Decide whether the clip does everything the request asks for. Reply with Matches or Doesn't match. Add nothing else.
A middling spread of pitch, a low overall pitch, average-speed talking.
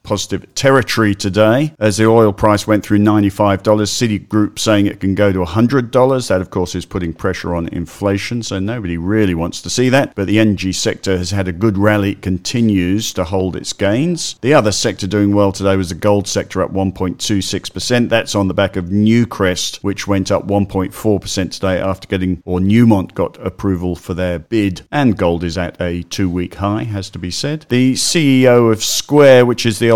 Matches